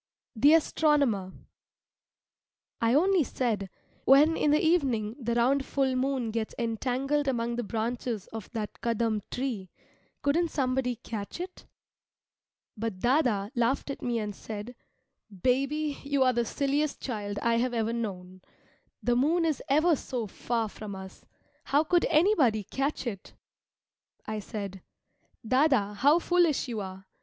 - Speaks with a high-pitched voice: Yes, high, 245 Hz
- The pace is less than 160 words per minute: Yes, average, 145 wpm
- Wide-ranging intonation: No, average, 4.5 semitones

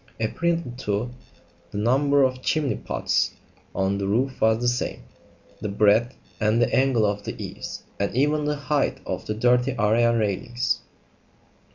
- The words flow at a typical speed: Yes, average, 150 wpm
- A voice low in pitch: Yes, low, 120 Hz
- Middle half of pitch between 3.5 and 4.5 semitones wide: Yes, average, 4.2 semitones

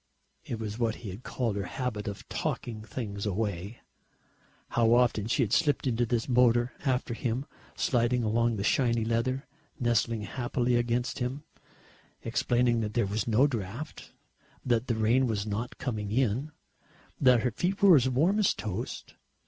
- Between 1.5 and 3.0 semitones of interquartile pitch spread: Yes, narrow, 2.5 semitones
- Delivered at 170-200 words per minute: No, average, 160 wpm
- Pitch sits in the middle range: No, low, 120 Hz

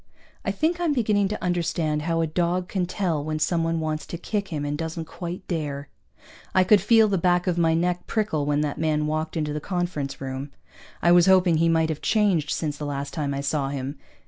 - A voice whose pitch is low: No, medium, 165 Hz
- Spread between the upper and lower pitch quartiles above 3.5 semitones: No, average, 3.2 semitones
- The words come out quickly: Yes, fast, 220 wpm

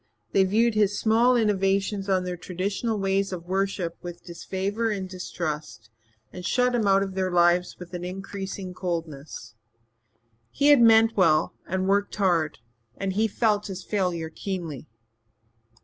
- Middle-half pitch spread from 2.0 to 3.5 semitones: Yes, narrow, 2.6 semitones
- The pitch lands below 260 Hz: Yes, high, 190 Hz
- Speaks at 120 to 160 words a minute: Yes, average, 150 wpm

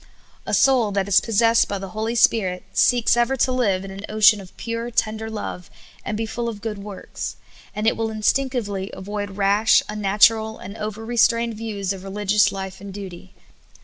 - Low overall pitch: No, high, 210 Hz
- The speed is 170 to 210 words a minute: Yes, average, 180 wpm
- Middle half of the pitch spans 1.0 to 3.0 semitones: Yes, narrow, 2.4 semitones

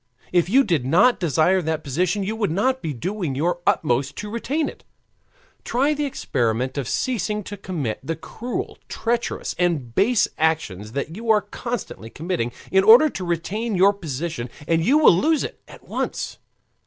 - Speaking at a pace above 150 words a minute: Yes, average, 170 wpm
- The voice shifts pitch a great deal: Yes, wide, 6.5 semitones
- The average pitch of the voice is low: No, medium, 180 Hz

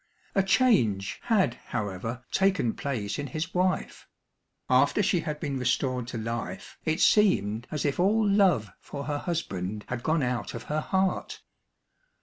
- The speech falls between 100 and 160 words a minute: Yes, average, 150 wpm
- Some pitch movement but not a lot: No, wide, 8.1 semitones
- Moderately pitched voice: Yes, medium, 145 Hz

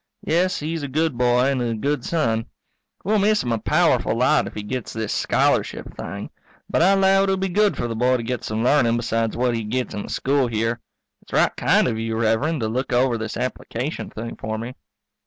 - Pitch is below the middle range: Yes, low, 125 Hz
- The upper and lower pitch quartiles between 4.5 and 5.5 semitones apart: Yes, average, 5.1 semitones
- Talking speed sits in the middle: No, fast, 220 wpm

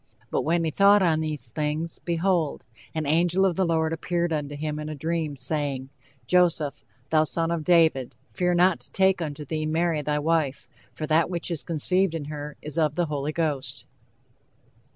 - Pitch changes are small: Yes, narrow, 2.3 semitones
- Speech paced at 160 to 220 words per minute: Yes, average, 185 wpm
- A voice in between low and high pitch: Yes, medium, 160 Hz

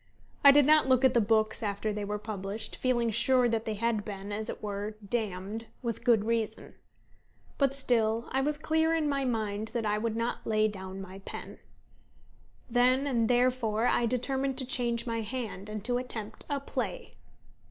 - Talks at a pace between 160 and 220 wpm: Yes, average, 185 wpm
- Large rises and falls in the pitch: No, average, 3.2 semitones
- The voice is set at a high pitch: Yes, high, 230 Hz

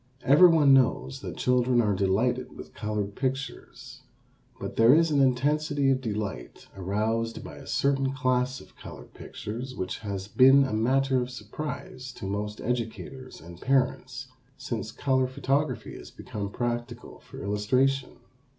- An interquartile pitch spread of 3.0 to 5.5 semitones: Yes, average, 3.9 semitones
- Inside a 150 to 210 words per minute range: No, average, 140 wpm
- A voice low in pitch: Yes, low, 125 Hz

